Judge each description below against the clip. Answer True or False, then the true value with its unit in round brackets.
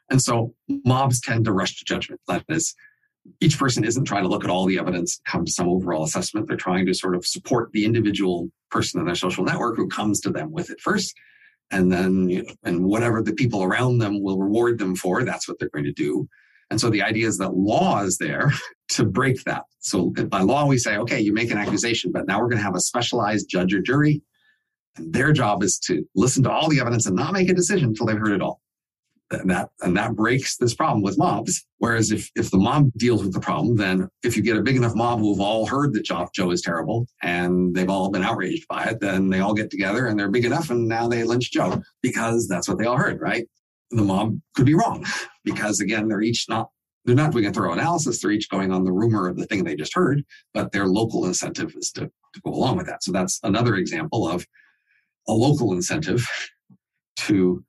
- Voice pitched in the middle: False (110 Hz)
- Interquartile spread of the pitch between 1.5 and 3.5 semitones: False (4.2 semitones)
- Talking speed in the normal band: False (235 wpm)